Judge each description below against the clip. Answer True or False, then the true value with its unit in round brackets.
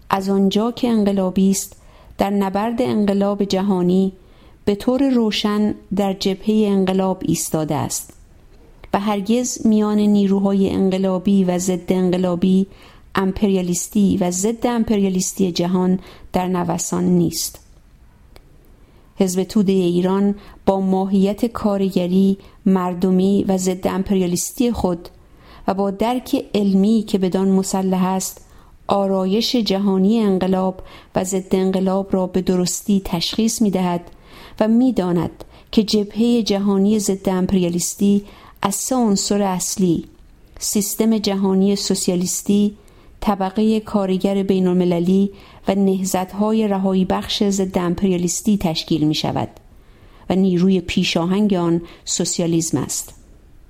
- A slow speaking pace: True (110 wpm)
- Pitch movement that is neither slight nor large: False (1.9 semitones)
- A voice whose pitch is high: True (195 Hz)